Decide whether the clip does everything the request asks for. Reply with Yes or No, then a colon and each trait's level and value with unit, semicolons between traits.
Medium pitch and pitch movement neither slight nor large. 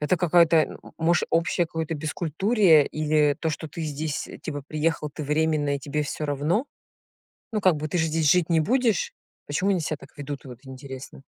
No: medium, 155 Hz; narrow, 2.3 semitones